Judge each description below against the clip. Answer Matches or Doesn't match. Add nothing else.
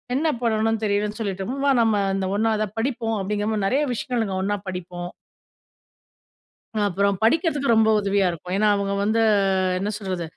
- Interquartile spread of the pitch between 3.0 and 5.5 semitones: Doesn't match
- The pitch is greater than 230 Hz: Doesn't match